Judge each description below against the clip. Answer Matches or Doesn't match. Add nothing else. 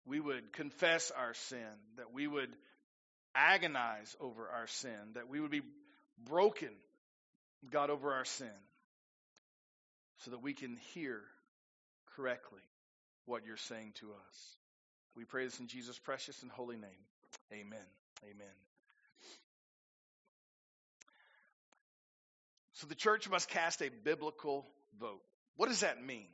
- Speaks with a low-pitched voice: Matches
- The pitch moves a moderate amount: Doesn't match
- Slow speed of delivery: Matches